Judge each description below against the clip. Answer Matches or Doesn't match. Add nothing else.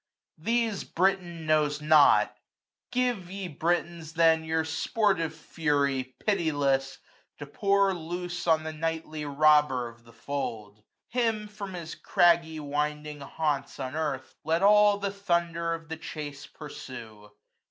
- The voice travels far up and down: Doesn't match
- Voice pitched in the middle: Matches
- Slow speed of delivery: Matches